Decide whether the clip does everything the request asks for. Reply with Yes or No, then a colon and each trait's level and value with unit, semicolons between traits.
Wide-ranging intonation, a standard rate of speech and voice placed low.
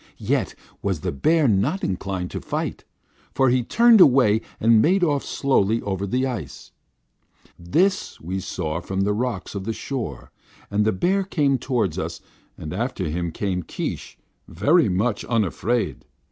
Yes: wide, 6.1 semitones; average, 155 wpm; low, 110 Hz